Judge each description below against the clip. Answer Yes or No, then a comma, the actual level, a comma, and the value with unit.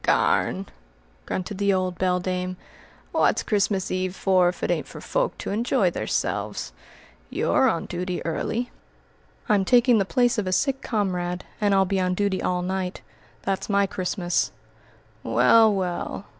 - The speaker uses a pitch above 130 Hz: Yes, high, 190 Hz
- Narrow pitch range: Yes, narrow, 2.2 semitones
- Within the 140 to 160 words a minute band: Yes, average, 150 wpm